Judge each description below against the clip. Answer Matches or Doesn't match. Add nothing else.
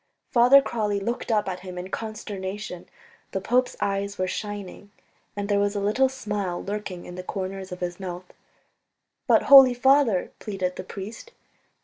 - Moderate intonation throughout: Matches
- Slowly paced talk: Doesn't match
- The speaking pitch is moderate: Doesn't match